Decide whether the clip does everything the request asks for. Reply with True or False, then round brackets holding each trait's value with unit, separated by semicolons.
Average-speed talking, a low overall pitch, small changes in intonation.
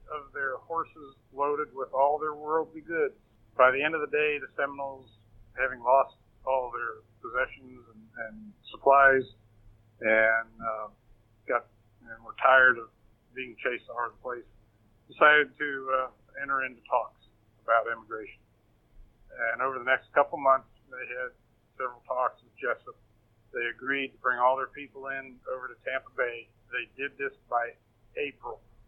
False (155 wpm; 130 Hz; 3.5 semitones)